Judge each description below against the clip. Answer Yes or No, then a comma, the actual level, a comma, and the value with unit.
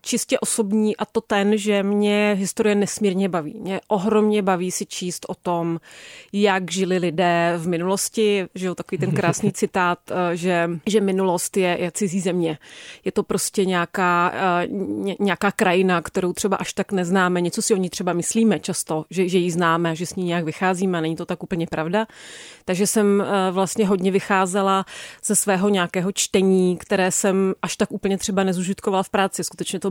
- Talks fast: Yes, fast, 175 wpm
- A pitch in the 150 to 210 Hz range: Yes, high, 190 Hz